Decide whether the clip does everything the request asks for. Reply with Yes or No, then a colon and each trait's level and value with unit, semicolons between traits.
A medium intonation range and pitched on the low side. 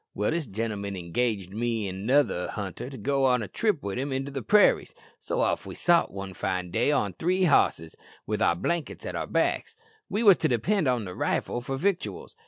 No: wide, 6.6 semitones; low, 120 Hz